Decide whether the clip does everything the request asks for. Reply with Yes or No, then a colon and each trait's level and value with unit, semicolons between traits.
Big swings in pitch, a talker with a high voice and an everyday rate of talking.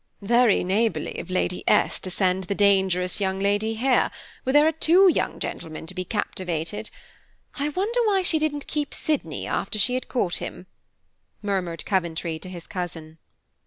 Yes: wide, 6.7 semitones; high, 200 Hz; average, 165 wpm